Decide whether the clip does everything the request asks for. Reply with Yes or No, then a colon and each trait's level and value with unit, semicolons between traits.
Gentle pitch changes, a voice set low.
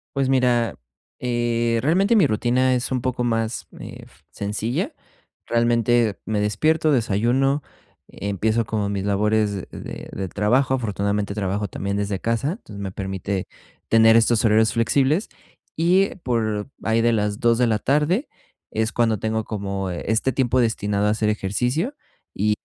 No: average, 3.4 semitones; low, 115 Hz